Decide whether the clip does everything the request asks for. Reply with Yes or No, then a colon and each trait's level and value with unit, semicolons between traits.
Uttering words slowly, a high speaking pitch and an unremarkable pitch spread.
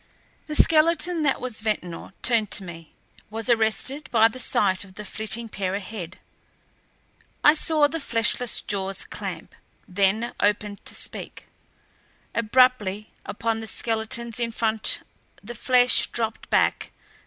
Yes: slow, 130 wpm; high, 225 Hz; average, 3.3 semitones